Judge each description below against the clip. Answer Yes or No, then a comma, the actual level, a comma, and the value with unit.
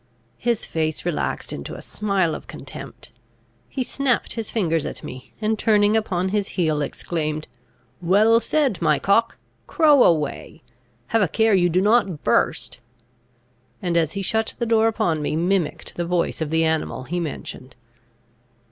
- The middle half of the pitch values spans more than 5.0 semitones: Yes, wide, 5.5 semitones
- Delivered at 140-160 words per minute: Yes, average, 155 wpm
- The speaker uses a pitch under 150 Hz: No, medium, 185 Hz